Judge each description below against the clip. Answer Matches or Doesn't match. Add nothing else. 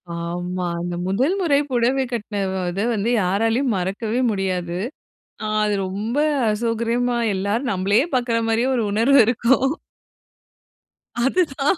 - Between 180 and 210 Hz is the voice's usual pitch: Doesn't match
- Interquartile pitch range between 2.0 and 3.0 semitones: Doesn't match